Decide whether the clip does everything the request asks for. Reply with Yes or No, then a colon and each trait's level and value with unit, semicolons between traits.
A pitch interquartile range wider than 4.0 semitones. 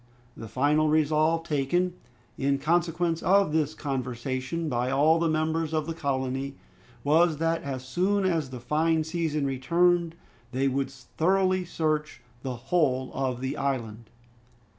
No: average, 3.7 semitones